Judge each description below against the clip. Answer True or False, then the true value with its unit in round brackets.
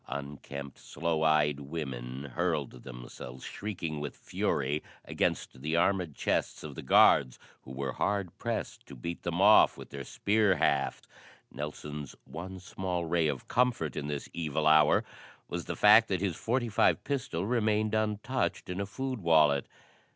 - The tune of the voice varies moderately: False (6.0 semitones)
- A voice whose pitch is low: True (80 Hz)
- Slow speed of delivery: False (150 wpm)